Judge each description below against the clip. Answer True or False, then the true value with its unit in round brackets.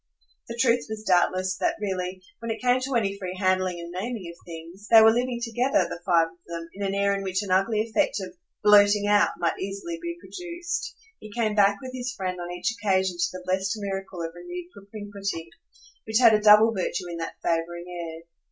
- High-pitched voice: True (200 Hz)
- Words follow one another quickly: True (210 wpm)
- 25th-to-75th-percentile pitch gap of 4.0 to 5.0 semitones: False (3.6 semitones)